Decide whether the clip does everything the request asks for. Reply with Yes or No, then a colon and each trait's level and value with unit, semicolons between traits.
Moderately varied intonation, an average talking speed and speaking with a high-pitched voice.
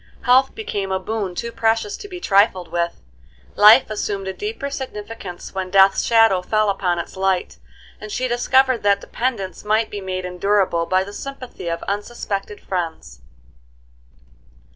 Yes: average, 3.4 semitones; average, 150 wpm; high, 200 Hz